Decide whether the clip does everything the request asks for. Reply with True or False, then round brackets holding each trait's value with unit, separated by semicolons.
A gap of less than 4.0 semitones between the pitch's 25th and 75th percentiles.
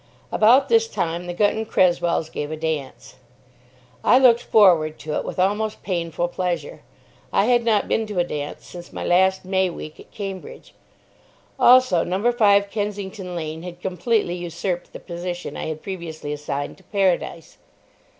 True (3.6 semitones)